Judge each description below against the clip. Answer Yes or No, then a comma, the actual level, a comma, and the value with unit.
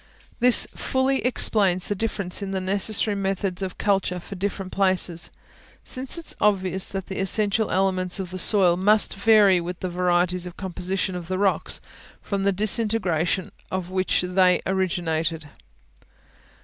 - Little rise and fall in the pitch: Yes, narrow, 1.9 semitones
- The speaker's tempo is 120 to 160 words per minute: Yes, average, 150 wpm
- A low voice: No, high, 190 Hz